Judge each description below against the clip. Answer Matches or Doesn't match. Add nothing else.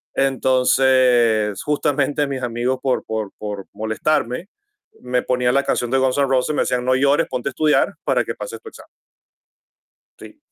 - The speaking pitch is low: Matches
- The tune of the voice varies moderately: Doesn't match